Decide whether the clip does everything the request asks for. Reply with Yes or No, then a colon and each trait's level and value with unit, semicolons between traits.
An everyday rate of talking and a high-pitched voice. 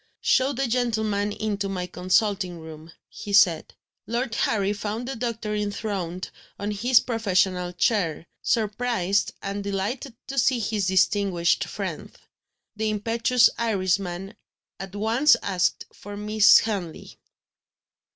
No: slow, 120 wpm; high, 205 Hz